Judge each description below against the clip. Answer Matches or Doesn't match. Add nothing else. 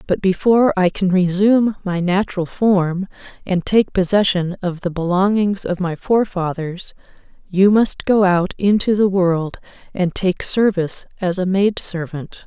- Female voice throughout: Matches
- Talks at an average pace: Matches